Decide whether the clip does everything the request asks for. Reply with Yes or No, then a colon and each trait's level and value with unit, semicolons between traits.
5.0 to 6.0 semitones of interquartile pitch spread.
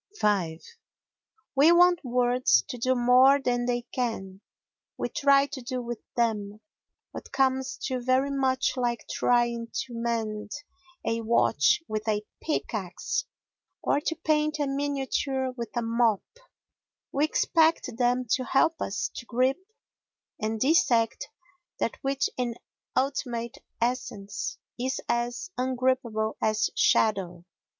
No: average, 3.0 semitones